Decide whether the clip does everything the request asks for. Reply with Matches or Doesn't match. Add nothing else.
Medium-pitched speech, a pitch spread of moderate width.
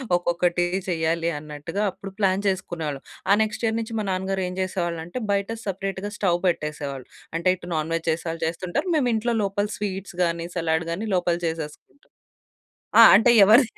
Matches